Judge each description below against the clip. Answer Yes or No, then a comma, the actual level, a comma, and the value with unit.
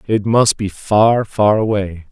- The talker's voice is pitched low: Yes, low, 105 Hz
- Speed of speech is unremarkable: Yes, average, 170 wpm